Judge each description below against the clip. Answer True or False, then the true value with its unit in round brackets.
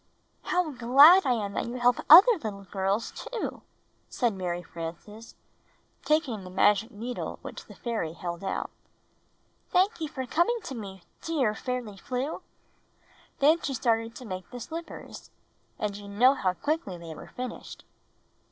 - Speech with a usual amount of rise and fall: False (6.3 semitones)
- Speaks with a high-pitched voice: True (235 Hz)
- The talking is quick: False (155 wpm)